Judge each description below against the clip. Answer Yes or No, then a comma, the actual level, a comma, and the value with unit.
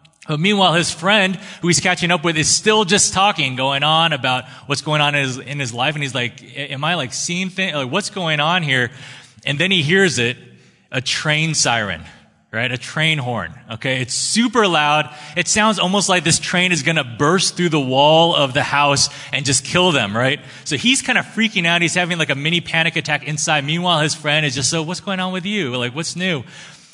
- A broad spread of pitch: No, average, 4.4 semitones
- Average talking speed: No, fast, 225 wpm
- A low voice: No, medium, 155 Hz